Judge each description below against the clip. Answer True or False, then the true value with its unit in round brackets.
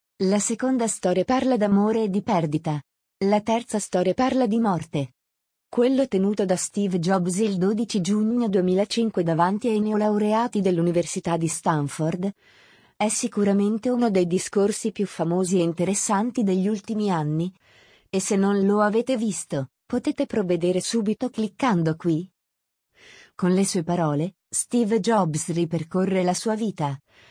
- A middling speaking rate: True (135 wpm)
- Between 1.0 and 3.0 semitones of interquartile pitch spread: False (4.1 semitones)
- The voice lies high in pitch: True (200 Hz)